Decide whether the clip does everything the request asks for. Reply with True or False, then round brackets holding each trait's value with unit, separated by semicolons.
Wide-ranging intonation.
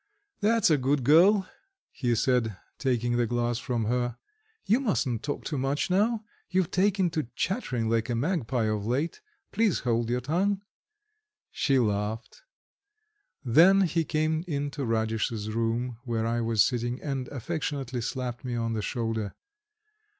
True (5.8 semitones)